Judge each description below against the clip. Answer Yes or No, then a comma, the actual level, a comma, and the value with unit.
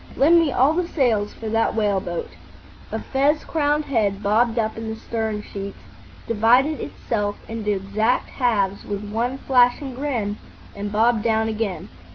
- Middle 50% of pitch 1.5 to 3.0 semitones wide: No, average, 3.7 semitones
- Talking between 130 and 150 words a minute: No, average, 160 wpm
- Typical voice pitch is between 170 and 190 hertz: No, high, 225 Hz